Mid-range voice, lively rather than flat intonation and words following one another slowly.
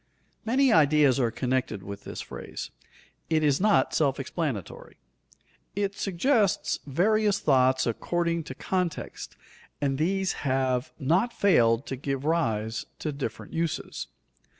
Yes: medium, 150 Hz; wide, 5.9 semitones; slow, 125 wpm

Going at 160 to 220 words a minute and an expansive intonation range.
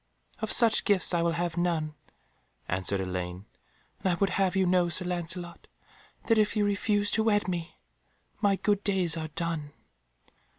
No: average, 165 wpm; average, 3.7 semitones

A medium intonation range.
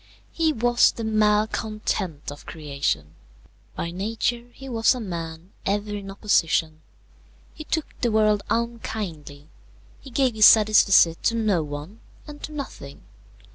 No: wide, 5.9 semitones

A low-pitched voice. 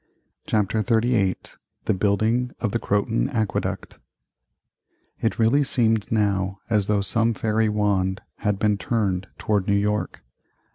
Yes: low, 105 Hz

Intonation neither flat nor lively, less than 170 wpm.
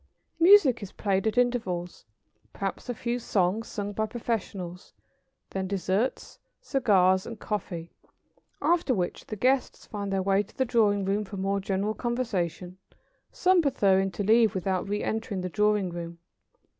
Yes: average, 3.5 semitones; average, 150 wpm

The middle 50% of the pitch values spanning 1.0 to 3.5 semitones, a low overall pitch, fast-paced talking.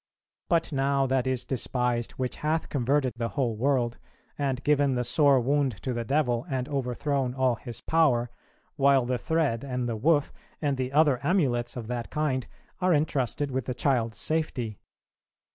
No: average, 2.9 semitones; low, 130 Hz; average, 165 wpm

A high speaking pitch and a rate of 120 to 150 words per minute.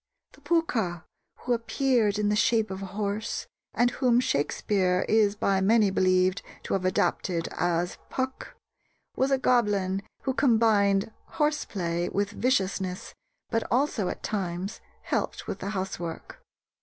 Yes: high, 205 Hz; average, 140 wpm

